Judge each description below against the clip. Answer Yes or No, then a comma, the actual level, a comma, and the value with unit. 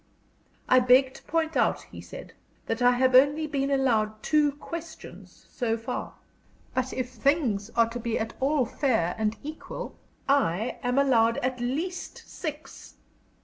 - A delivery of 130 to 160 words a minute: Yes, average, 150 wpm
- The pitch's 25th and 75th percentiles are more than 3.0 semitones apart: Yes, average, 3.8 semitones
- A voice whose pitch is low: No, very high, 255 Hz